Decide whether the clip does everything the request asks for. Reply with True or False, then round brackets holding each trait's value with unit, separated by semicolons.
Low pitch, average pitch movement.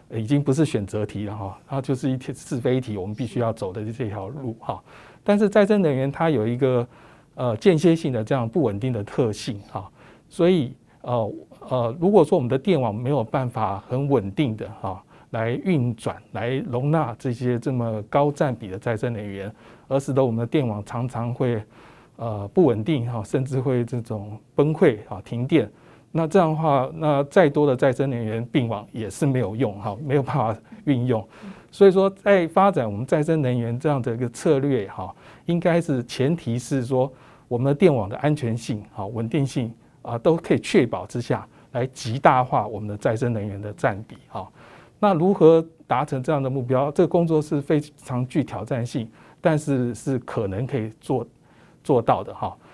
True (130 Hz; 4.5 semitones)